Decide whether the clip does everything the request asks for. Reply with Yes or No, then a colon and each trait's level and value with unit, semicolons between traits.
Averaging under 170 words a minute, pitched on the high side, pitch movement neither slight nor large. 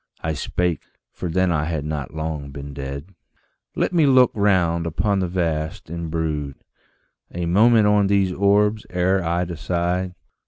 No: average, 155 wpm; very low, 85 Hz; average, 3.7 semitones